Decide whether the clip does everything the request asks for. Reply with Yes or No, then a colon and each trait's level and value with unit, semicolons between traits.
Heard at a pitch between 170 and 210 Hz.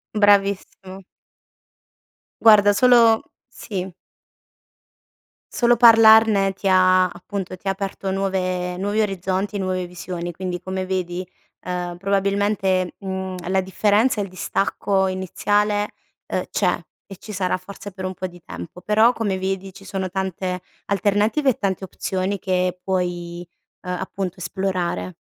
Yes: high, 190 Hz